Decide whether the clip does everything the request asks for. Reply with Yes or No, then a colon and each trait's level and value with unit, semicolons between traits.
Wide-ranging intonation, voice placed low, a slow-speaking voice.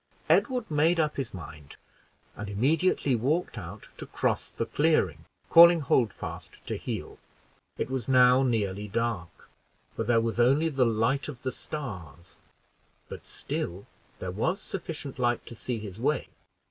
No: wide, 6.1 semitones; low, 120 Hz; average, 145 wpm